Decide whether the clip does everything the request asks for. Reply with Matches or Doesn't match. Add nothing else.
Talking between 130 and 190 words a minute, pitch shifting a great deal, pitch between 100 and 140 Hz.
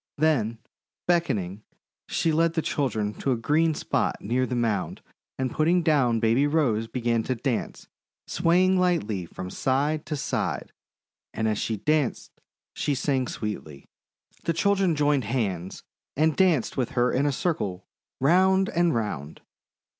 Matches